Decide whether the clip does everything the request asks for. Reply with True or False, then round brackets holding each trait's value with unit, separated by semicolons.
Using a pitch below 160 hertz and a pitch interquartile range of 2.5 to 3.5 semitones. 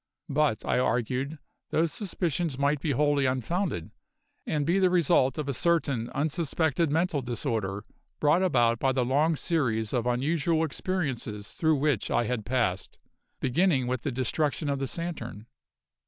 False (140 Hz; 4.6 semitones)